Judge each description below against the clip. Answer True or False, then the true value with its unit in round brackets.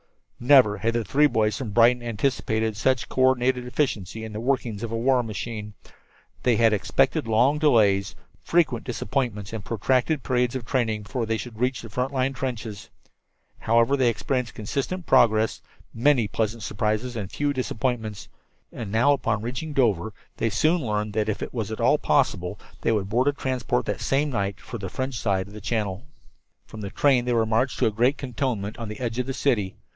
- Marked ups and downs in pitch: False (3.3 semitones)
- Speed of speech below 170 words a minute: False (190 wpm)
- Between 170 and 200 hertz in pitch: False (115 Hz)